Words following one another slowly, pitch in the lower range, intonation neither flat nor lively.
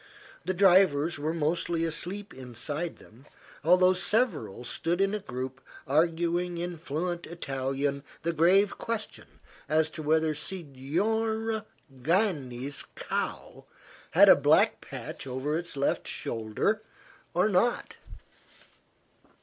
No: slow, 110 wpm; medium, 165 Hz; average, 4.6 semitones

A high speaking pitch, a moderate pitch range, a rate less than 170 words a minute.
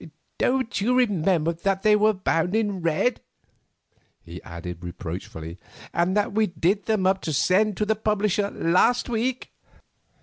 Yes: high, 195 Hz; average, 4.6 semitones; average, 145 wpm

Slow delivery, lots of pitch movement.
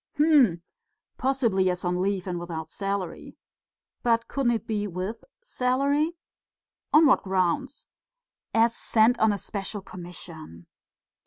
Yes: slow, 120 wpm; wide, 5.7 semitones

